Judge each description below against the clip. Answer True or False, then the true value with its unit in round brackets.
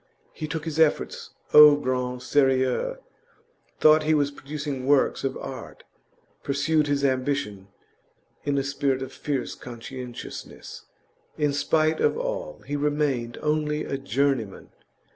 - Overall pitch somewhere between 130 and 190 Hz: True (140 Hz)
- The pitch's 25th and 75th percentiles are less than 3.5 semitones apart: True (2.5 semitones)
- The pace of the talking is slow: True (125 wpm)